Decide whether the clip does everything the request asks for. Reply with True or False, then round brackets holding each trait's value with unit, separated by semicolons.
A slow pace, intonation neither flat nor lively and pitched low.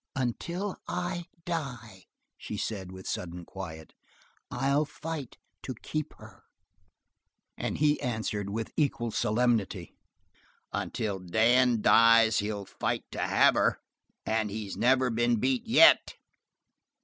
True (115 wpm; 4.7 semitones; 115 Hz)